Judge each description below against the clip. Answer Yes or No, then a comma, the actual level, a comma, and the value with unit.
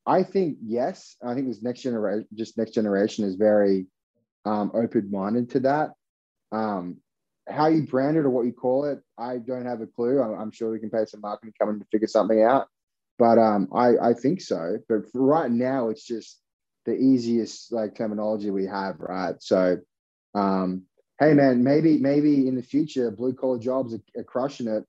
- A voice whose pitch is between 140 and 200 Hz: No, low, 115 Hz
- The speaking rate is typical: Yes, average, 190 wpm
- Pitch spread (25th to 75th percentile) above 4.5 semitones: No, average, 3.5 semitones